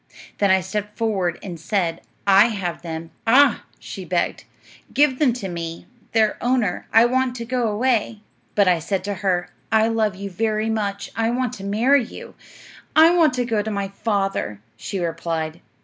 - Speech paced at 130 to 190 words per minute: Yes, average, 180 wpm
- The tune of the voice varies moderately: Yes, average, 3.7 semitones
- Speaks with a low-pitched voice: No, high, 210 Hz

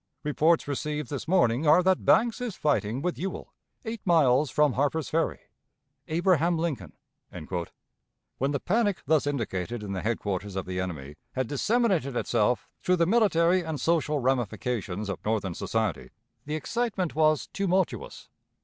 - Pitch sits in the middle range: Yes, medium, 150 Hz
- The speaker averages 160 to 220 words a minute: No, average, 145 wpm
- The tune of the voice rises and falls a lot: Yes, wide, 7.0 semitones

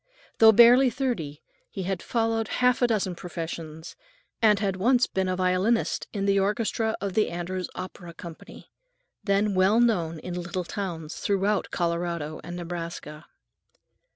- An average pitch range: Yes, average, 4.3 semitones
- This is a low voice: No, high, 190 Hz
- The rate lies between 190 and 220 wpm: No, average, 145 wpm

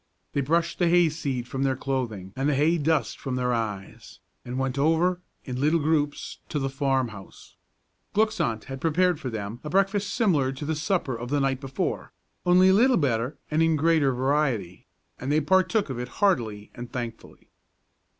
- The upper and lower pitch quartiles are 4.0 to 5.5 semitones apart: Yes, average, 4.7 semitones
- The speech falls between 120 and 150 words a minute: No, average, 190 wpm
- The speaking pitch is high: No, medium, 140 Hz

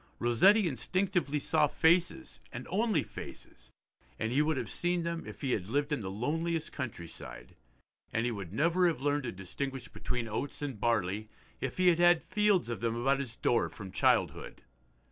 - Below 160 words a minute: No, average, 180 wpm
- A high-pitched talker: No, medium, 140 Hz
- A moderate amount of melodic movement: No, wide, 6.5 semitones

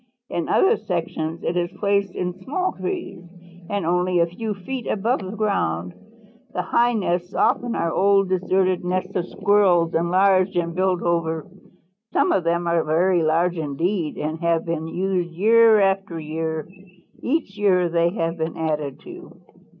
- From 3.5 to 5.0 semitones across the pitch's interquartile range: No, average, 2.9 semitones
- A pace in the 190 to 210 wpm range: No, average, 160 wpm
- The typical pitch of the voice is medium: Yes, medium, 180 Hz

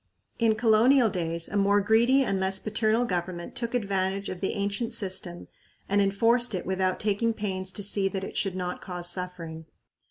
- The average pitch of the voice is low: No, high, 195 Hz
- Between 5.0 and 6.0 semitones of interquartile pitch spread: No, average, 3.0 semitones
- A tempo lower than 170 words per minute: No, average, 180 wpm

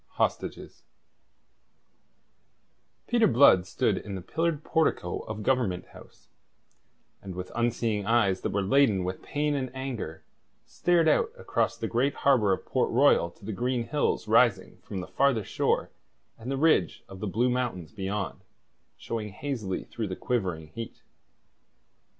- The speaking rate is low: No, average, 145 wpm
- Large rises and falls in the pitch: Yes, wide, 5.8 semitones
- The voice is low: Yes, low, 115 Hz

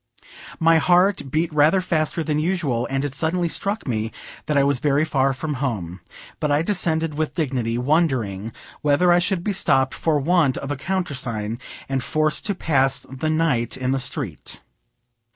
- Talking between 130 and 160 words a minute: No, average, 170 wpm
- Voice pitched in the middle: Yes, medium, 150 Hz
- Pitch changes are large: No, average, 3.9 semitones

